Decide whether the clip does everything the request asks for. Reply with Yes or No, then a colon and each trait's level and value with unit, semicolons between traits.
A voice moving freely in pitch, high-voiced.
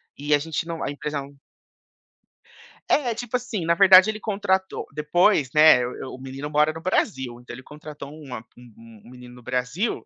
No: wide, 6.3 semitones; medium, 150 Hz